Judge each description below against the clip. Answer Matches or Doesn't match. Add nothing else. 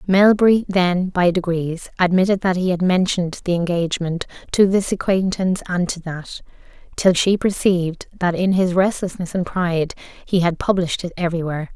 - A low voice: Doesn't match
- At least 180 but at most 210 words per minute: Doesn't match